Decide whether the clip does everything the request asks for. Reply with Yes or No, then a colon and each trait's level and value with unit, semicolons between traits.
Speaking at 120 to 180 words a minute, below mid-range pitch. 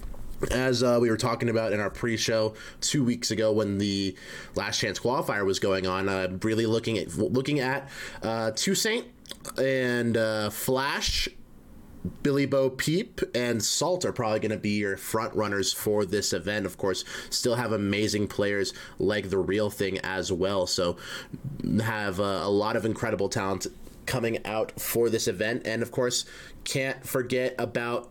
Yes: average, 170 wpm; low, 110 Hz